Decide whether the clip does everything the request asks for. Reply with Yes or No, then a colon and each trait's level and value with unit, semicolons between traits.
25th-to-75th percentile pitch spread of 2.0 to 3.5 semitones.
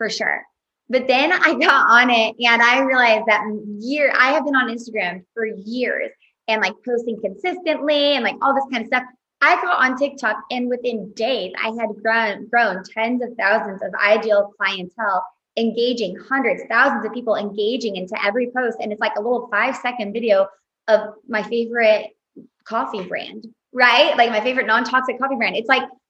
Yes: average, 3.0 semitones